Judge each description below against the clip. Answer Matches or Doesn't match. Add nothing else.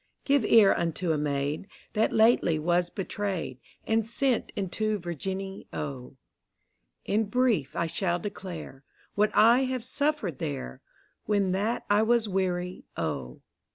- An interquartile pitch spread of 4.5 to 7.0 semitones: Matches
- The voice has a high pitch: Matches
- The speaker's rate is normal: Doesn't match